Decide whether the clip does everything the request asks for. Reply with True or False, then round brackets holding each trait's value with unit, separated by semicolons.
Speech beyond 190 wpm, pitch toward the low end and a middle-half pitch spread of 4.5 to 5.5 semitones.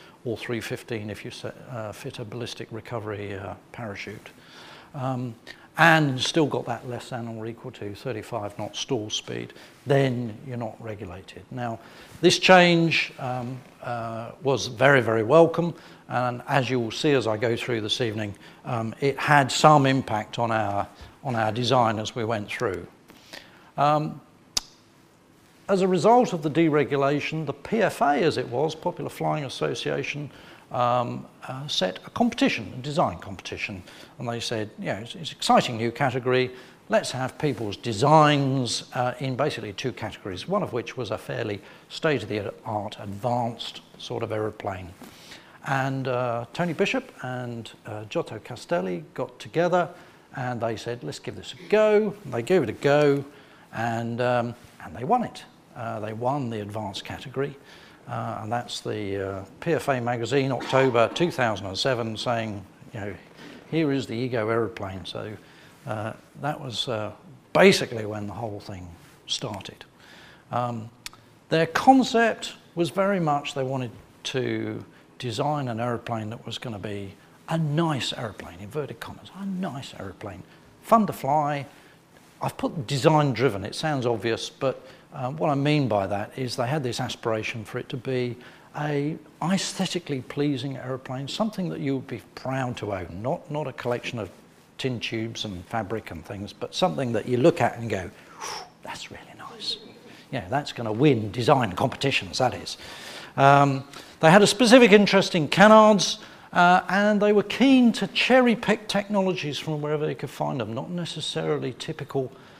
False (165 wpm; 130 Hz; 5.0 semitones)